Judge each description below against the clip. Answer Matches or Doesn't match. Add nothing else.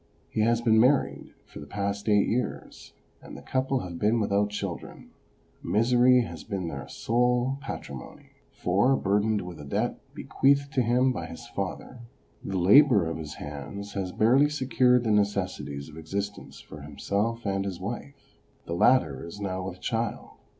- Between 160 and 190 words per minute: Matches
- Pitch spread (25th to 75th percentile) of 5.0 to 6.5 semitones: Matches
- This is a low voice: Matches